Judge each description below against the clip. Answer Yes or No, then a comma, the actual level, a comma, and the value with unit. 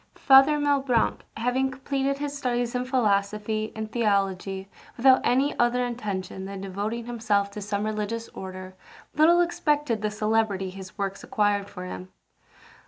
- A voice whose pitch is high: Yes, high, 220 Hz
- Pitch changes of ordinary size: Yes, average, 4.6 semitones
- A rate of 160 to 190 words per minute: No, average, 140 wpm